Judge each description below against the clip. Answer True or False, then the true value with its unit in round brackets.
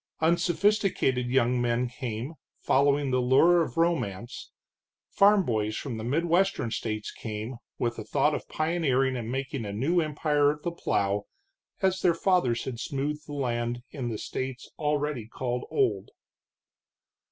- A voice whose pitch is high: False (135 Hz)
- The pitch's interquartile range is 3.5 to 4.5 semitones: False (5.2 semitones)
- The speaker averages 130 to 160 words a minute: True (145 wpm)